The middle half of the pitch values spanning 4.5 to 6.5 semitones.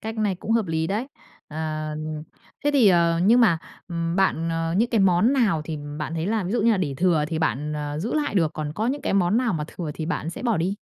Yes: wide, 5.4 semitones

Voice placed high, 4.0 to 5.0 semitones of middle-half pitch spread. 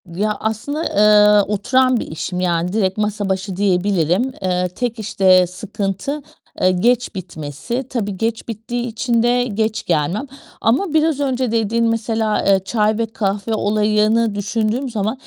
No: high, 215 Hz; average, 3.3 semitones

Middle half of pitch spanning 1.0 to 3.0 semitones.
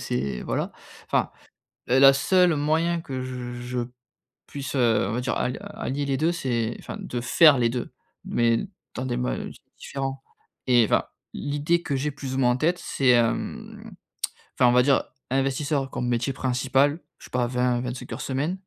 Yes: narrow, 2.5 semitones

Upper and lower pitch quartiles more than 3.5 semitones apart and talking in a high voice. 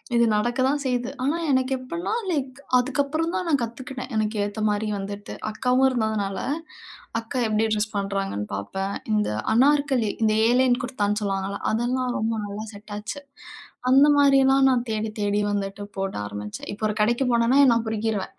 Yes: average, 4.1 semitones; high, 225 Hz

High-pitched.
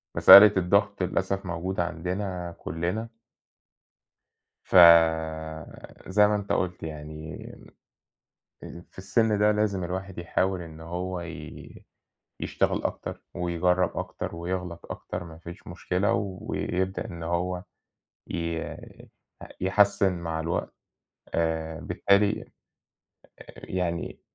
No: very low, 90 Hz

